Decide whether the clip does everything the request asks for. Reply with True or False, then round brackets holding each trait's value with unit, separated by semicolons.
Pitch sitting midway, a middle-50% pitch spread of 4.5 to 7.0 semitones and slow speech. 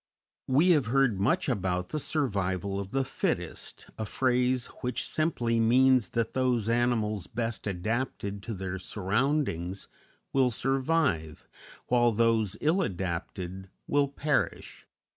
False (115 Hz; 5.1 semitones; 125 wpm)